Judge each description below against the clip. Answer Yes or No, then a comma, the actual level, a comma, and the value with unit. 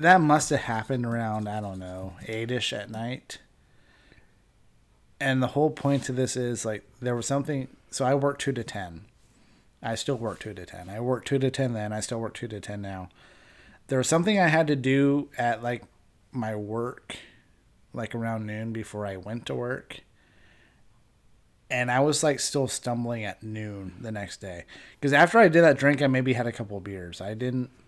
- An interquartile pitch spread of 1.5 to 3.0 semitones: No, average, 4.2 semitones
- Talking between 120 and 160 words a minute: No, average, 200 wpm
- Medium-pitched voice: No, low, 120 Hz